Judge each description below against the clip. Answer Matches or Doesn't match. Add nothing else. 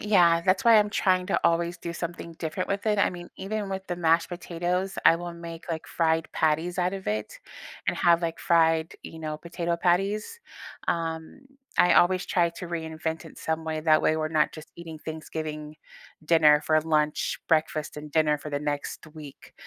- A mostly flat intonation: Matches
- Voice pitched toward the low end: Doesn't match